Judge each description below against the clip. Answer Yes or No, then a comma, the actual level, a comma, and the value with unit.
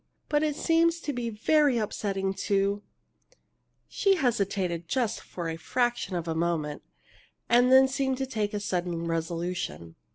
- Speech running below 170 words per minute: Yes, average, 150 wpm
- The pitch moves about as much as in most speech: No, wide, 7.3 semitones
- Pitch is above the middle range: Yes, high, 205 Hz